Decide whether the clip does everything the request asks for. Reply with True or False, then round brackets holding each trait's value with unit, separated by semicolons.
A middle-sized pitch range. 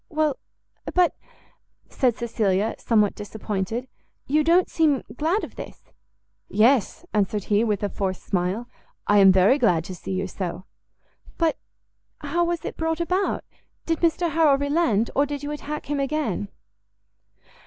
False (7.4 semitones)